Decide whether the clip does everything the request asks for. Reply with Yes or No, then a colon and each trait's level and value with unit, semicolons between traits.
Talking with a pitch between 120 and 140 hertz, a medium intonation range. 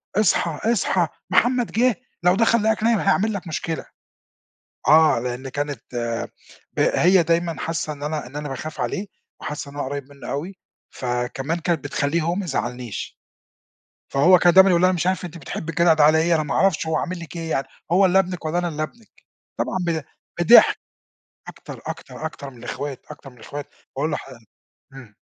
No: medium, 160 Hz; average, 4.1 semitones